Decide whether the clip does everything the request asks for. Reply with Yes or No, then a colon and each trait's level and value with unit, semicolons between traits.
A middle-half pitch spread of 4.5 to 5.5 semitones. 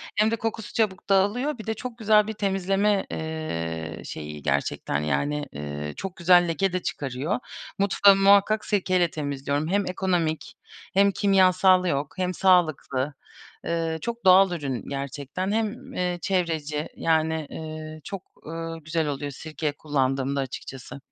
Yes: average, 5.2 semitones